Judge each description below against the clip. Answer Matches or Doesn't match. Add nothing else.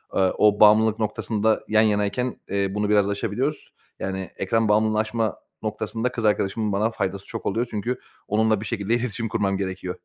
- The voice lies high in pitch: Doesn't match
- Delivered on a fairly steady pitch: Matches